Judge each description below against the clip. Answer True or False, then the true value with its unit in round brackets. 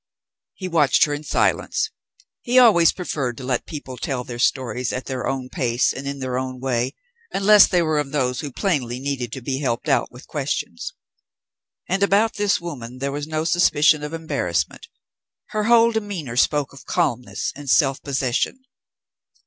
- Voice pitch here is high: False (140 Hz)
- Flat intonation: False (5.0 semitones)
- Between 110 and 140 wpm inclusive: False (175 wpm)